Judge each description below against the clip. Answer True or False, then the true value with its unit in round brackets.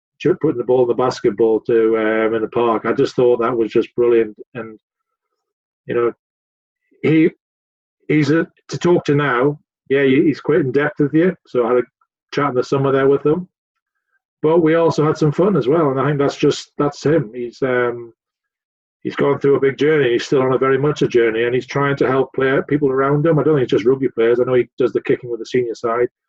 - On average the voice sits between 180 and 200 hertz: False (135 Hz)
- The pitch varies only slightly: False (4.0 semitones)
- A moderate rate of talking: False (235 wpm)